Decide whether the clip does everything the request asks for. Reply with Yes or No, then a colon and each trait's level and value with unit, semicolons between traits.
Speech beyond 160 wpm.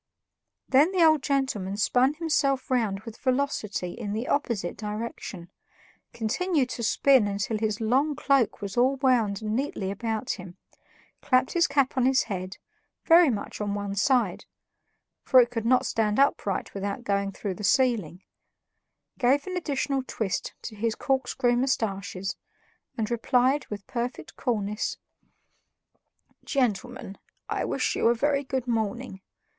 No: average, 140 wpm